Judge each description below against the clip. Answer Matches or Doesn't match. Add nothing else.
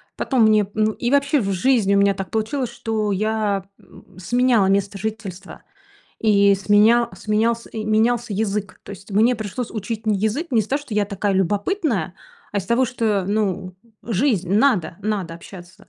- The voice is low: Doesn't match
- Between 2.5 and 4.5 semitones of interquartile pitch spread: Matches